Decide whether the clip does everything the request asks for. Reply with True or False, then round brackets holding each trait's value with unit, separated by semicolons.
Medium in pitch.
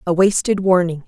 True (180 Hz)